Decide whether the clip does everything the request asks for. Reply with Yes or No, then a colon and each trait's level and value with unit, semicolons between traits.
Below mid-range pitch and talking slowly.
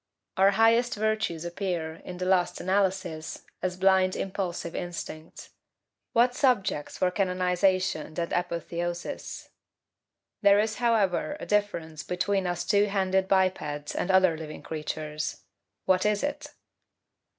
No: medium, 185 Hz; slow, 120 wpm